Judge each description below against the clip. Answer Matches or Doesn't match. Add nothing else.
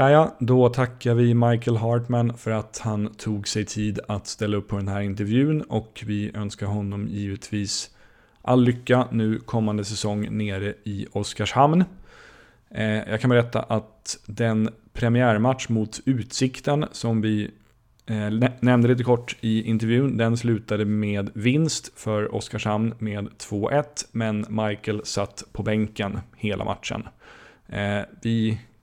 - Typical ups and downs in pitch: Doesn't match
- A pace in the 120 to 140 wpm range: Matches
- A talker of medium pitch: Doesn't match